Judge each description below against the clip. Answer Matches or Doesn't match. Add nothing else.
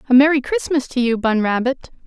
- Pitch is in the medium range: Doesn't match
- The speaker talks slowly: Doesn't match